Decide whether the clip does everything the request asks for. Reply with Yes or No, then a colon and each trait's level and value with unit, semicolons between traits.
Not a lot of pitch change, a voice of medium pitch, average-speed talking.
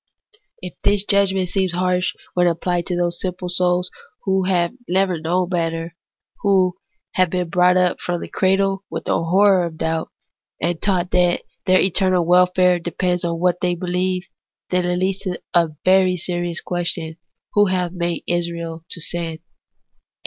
Yes: narrow, 1.3 semitones; medium, 180 Hz; average, 160 wpm